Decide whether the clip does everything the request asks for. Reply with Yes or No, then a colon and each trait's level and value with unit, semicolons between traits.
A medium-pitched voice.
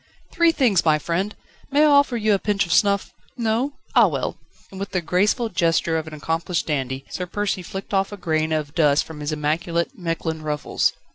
Yes: medium, 175 Hz